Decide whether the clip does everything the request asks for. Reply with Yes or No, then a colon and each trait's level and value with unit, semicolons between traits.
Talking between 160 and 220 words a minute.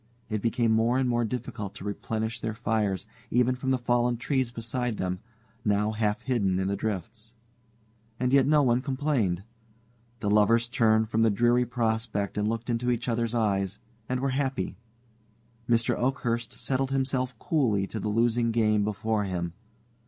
Yes: average, 165 wpm